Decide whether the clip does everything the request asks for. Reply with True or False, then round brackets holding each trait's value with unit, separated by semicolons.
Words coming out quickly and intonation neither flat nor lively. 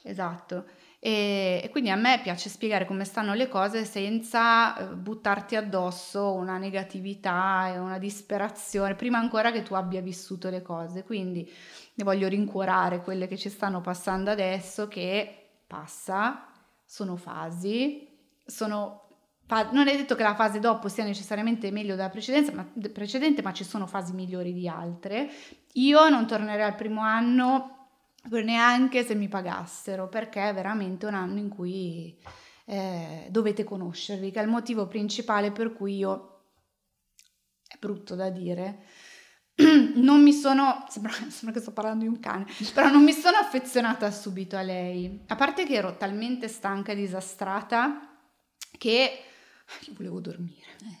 False (145 wpm; 3.4 semitones)